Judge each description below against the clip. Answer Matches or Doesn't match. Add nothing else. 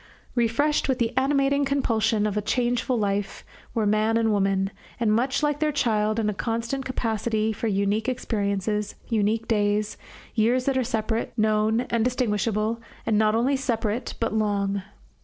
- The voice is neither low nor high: Doesn't match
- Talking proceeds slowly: Doesn't match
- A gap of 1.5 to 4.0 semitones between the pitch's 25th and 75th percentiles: Matches